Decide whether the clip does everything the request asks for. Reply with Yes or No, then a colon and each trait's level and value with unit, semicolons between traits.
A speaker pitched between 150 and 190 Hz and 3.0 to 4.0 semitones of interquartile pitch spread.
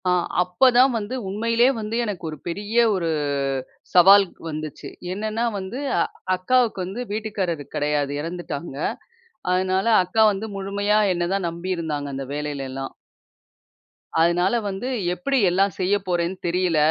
Yes: medium, 185 Hz; average, 3.6 semitones